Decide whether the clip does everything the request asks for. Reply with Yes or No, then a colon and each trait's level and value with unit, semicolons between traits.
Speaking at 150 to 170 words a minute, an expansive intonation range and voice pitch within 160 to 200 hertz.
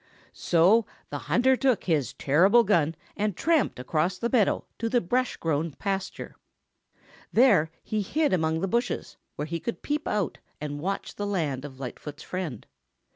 Yes: average, 160 wpm; wide, 6.9 semitones; medium, 185 Hz